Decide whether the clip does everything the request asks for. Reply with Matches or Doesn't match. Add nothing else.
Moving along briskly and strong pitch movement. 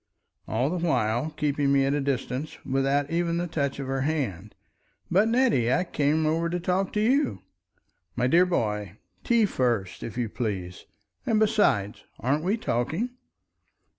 Doesn't match